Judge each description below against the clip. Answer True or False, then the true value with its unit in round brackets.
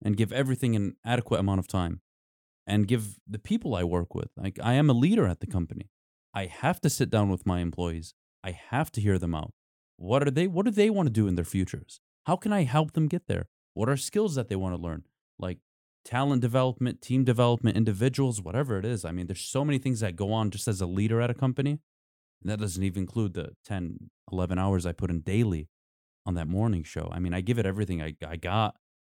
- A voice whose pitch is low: True (105 Hz)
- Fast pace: True (240 wpm)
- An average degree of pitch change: False (6.2 semitones)